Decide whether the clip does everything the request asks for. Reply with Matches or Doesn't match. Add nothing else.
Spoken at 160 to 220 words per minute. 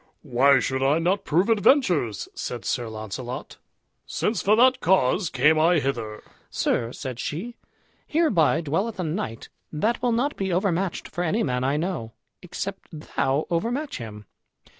Doesn't match